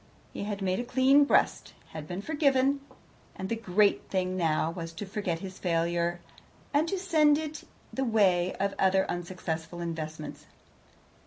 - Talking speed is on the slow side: No, average, 155 wpm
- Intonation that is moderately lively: No, wide, 7.0 semitones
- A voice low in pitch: No, high, 190 Hz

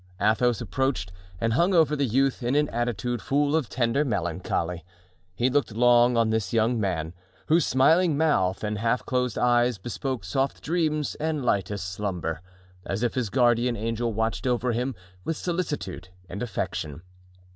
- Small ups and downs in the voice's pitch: No, average, 4.7 semitones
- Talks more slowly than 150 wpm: No, average, 155 wpm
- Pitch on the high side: No, low, 120 Hz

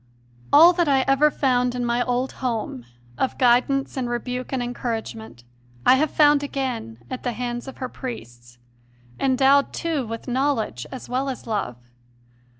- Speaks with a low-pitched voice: No, very high, 250 Hz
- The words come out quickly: No, average, 155 wpm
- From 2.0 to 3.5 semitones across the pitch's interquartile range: Yes, narrow, 2.4 semitones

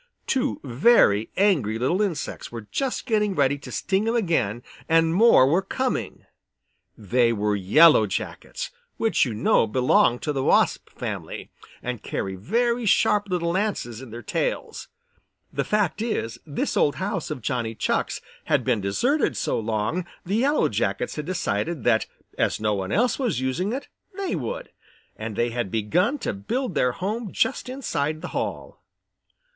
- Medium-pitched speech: Yes, medium, 155 Hz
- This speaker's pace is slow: No, average, 160 wpm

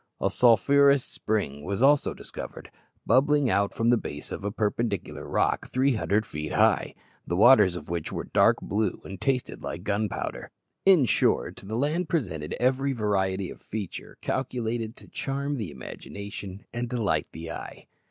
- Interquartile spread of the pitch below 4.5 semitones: No, wide, 5.4 semitones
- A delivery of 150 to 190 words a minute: Yes, average, 160 wpm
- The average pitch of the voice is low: Yes, low, 110 Hz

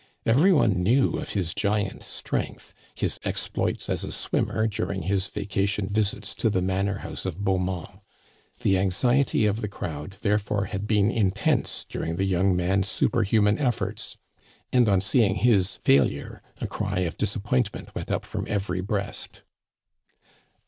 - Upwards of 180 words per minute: No, average, 155 wpm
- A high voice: No, low, 100 Hz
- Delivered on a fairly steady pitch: Yes, narrow, 2.3 semitones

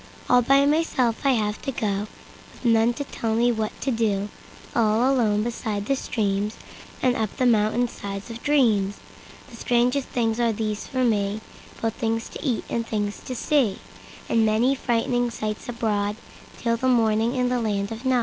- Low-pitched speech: No, high, 230 Hz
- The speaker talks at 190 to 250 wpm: No, average, 155 wpm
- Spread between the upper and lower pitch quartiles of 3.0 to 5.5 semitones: No, narrow, 2.6 semitones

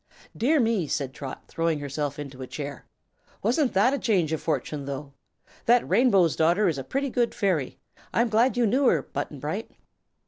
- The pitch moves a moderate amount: No, wide, 8.5 semitones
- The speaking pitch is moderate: Yes, medium, 175 Hz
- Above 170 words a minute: Yes, average, 185 wpm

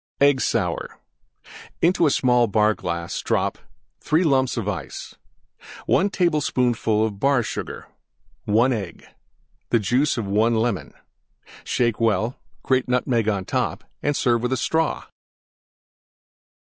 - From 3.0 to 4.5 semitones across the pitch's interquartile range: Yes, average, 3.7 semitones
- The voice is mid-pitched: No, low, 120 Hz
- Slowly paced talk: Yes, slow, 105 wpm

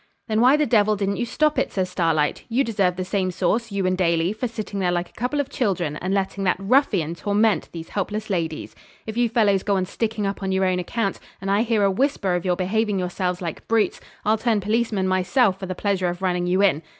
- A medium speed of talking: No, fast, 235 wpm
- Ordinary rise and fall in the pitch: Yes, average, 3.2 semitones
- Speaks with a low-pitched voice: No, high, 195 Hz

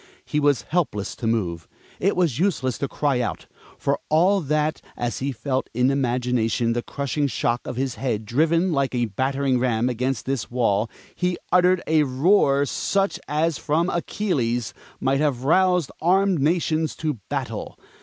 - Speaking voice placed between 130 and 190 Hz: Yes, medium, 140 Hz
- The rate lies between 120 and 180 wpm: Yes, average, 160 wpm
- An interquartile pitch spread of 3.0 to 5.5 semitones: Yes, average, 4.9 semitones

